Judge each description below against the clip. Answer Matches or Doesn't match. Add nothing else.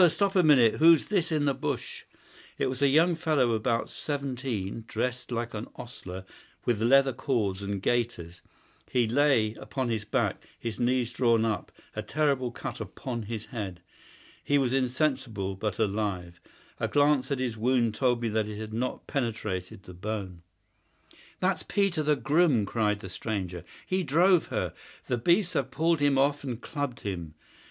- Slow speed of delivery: Doesn't match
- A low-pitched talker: Matches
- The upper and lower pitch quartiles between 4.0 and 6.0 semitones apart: Matches